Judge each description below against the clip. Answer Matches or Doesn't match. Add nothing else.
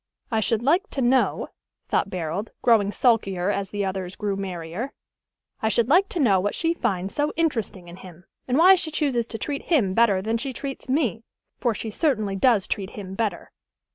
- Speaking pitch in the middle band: Doesn't match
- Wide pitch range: Matches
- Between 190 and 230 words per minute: Matches